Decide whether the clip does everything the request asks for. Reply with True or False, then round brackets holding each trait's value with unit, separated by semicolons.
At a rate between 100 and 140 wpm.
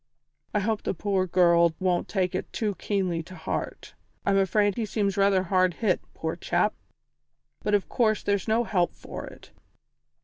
False (170 wpm)